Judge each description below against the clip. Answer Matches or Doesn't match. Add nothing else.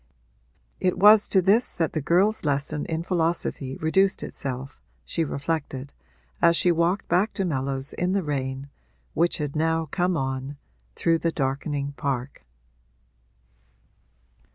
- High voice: Doesn't match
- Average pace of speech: Doesn't match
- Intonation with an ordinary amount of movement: Matches